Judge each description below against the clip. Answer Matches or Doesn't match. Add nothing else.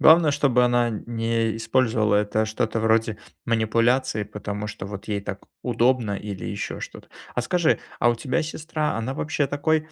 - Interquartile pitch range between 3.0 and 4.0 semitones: Matches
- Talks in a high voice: Doesn't match